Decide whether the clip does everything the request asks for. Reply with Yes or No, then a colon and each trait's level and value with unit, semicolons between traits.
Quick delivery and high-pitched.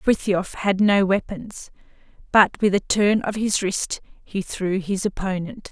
No: average, 160 wpm; high, 195 Hz